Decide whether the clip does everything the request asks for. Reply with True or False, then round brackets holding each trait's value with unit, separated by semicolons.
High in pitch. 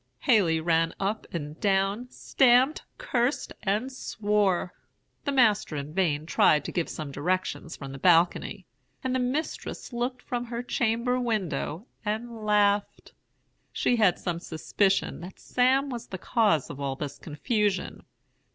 True (205 Hz)